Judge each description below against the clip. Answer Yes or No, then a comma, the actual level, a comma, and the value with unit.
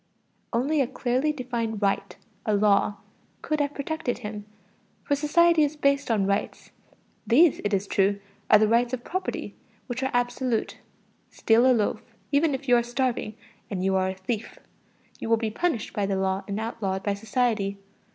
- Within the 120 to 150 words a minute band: No, average, 175 wpm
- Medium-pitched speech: No, high, 235 Hz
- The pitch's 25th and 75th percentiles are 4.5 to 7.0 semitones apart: Yes, average, 4.8 semitones